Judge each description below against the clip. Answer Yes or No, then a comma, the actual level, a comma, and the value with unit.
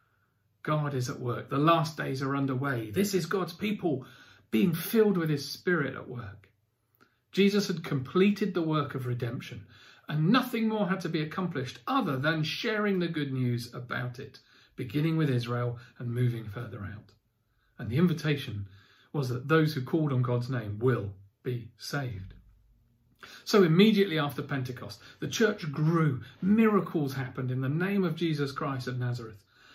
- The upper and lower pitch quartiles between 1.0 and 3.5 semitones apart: No, wide, 5.4 semitones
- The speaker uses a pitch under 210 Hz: Yes, low, 135 Hz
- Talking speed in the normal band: Yes, average, 160 wpm